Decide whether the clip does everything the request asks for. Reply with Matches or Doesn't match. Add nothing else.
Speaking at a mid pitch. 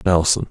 Doesn't match